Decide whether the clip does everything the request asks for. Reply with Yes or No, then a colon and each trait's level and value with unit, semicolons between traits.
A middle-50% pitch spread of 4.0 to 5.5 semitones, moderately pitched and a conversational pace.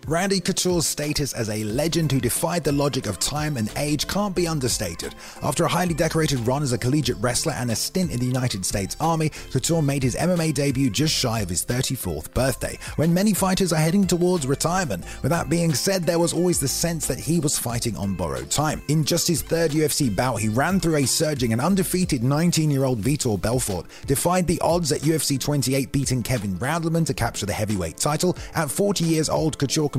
No: average, 4.9 semitones; medium, 145 Hz; fast, 210 wpm